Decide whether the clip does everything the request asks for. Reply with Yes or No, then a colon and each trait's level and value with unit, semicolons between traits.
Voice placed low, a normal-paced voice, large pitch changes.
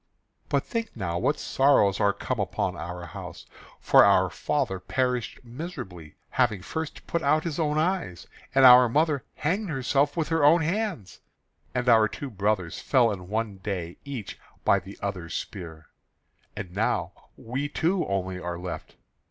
Yes: low, 120 Hz; average, 160 wpm; wide, 7.9 semitones